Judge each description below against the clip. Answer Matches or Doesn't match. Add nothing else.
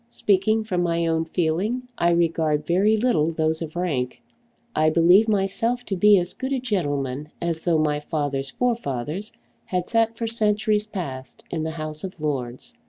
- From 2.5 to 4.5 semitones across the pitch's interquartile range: Doesn't match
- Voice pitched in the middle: Matches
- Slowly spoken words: Doesn't match